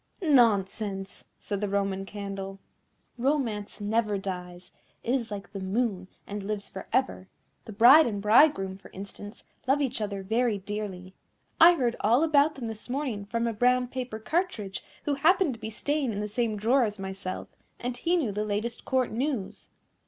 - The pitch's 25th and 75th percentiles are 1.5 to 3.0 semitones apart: No, average, 4.1 semitones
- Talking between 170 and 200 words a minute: Yes, average, 175 wpm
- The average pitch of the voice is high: Yes, high, 215 Hz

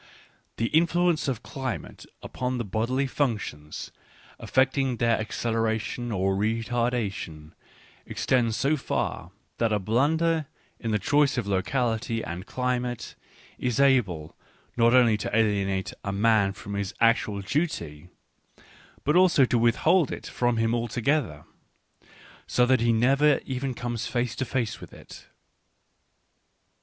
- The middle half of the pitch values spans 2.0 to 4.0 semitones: Yes, average, 3.7 semitones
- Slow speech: Yes, slow, 130 wpm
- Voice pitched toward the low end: Yes, low, 120 Hz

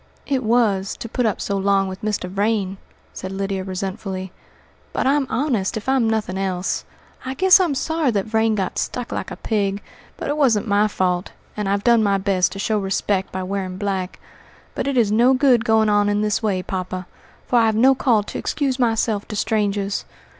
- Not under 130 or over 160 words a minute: No, average, 195 wpm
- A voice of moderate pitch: No, high, 210 Hz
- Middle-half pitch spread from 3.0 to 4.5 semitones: Yes, average, 3.3 semitones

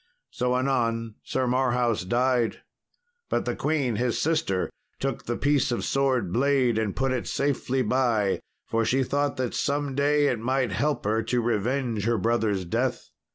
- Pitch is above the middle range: No, low, 125 Hz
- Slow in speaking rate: No, average, 160 wpm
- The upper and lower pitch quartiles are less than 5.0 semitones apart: Yes, average, 3.0 semitones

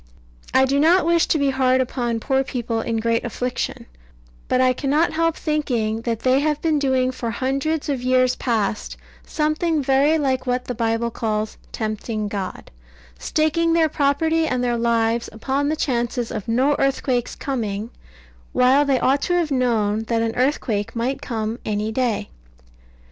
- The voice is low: No, very high, 255 Hz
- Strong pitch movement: No, average, 3.7 semitones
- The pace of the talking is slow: No, average, 165 wpm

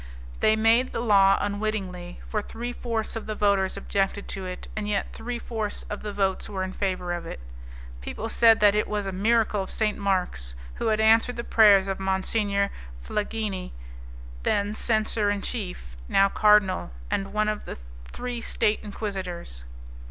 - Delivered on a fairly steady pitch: Yes, narrow, 2.2 semitones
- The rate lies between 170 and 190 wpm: Yes, average, 175 wpm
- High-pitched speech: Yes, high, 205 Hz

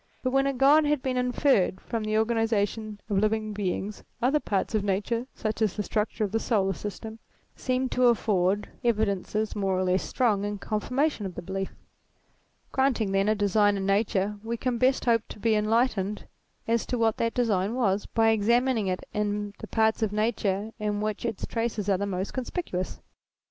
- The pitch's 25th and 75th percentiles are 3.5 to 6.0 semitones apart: No, narrow, 2.6 semitones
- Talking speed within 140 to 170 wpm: No, average, 190 wpm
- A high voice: Yes, high, 215 Hz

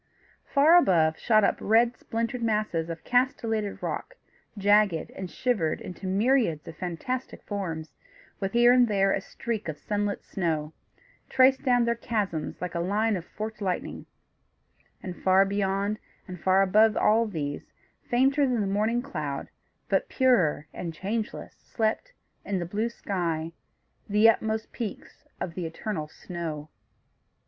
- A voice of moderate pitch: No, high, 205 Hz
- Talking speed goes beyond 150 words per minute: No, average, 145 wpm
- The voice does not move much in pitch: No, average, 5.0 semitones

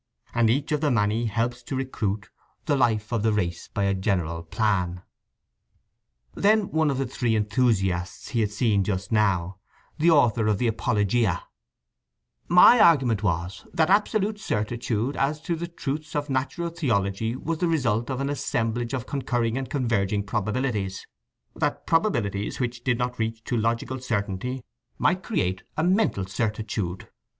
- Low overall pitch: Yes, low, 115 Hz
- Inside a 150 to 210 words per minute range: Yes, average, 155 wpm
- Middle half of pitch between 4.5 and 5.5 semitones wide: Yes, average, 5.1 semitones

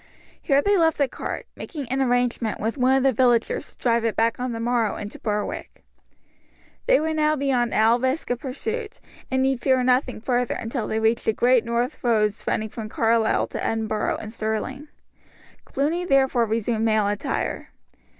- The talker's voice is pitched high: Yes, high, 245 Hz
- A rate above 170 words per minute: Yes, average, 180 wpm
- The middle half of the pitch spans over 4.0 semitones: No, average, 3.2 semitones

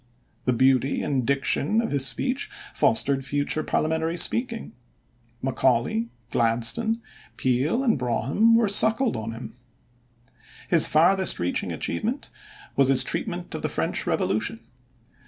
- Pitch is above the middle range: No, medium, 140 Hz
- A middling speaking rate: No, slow, 120 wpm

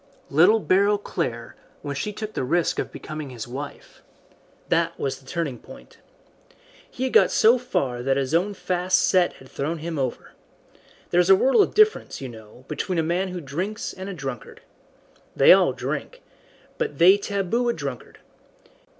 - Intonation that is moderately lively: No, wide, 6.7 semitones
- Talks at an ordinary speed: Yes, average, 175 wpm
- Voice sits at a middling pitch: Yes, medium, 175 Hz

